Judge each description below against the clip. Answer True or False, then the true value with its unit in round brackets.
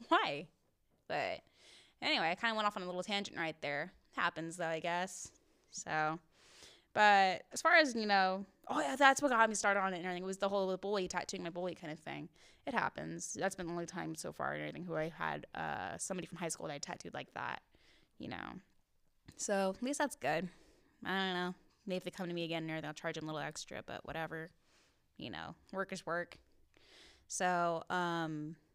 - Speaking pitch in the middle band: True (180 Hz)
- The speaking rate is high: True (220 wpm)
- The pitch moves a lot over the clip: False (3.1 semitones)